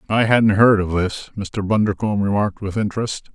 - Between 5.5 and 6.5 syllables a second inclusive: Yes, 5.7 syllables/s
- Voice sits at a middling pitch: No, low, 100 Hz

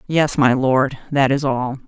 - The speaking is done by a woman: Yes, female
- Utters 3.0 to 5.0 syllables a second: Yes, 3.8 syllables/s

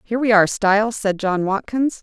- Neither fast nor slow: No, fast, 210 wpm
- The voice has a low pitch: No, high, 215 Hz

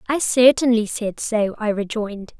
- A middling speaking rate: Yes, average, 150 wpm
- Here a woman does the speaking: Yes, female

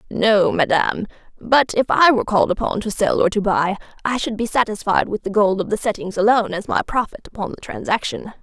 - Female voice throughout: Yes, female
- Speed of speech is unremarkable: No, fast, 215 wpm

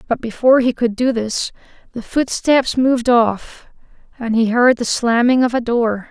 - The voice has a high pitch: Yes, high, 240 Hz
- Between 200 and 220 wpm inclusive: No, average, 175 wpm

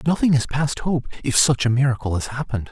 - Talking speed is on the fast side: Yes, fast, 220 wpm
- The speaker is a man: Yes, male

